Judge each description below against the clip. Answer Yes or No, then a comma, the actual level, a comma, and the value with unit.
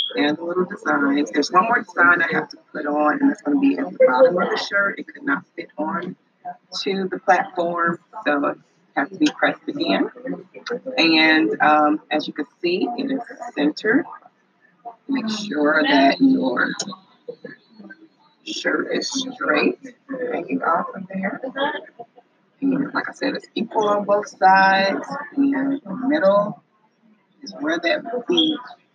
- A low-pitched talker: No, high, 240 Hz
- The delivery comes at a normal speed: Yes, average, 160 wpm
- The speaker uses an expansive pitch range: Yes, wide, 6.9 semitones